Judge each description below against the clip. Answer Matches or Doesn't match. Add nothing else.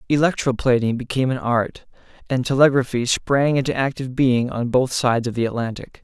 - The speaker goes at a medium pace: Matches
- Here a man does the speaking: Matches